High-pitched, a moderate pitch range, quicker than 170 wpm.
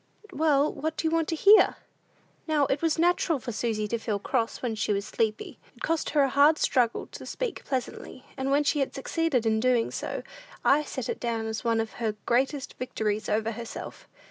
Yes: very high, 255 Hz; average, 5.0 semitones; average, 200 wpm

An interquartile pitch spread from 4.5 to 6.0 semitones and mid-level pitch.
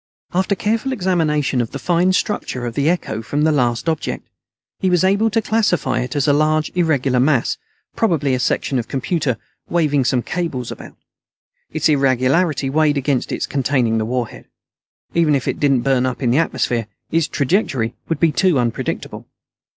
Yes: average, 5.1 semitones; medium, 145 Hz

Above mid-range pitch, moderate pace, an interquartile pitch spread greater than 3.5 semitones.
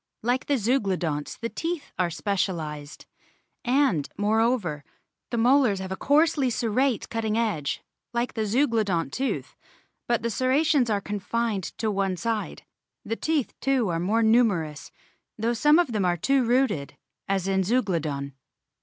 Yes: high, 220 Hz; average, 145 wpm; average, 5.1 semitones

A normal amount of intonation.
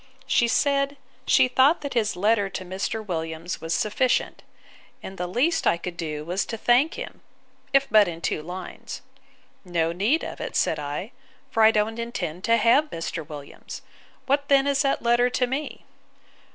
No: wide, 6.9 semitones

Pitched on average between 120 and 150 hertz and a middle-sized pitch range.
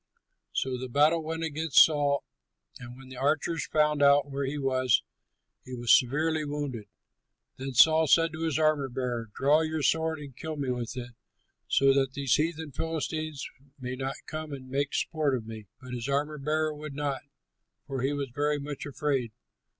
Yes: medium, 140 Hz; average, 3.0 semitones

